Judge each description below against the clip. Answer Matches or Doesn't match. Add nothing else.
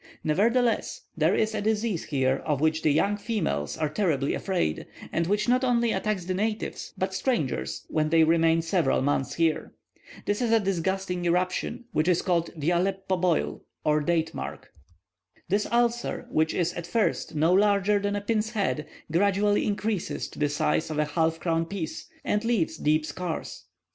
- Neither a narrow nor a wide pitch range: Matches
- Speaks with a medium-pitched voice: Matches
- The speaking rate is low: Doesn't match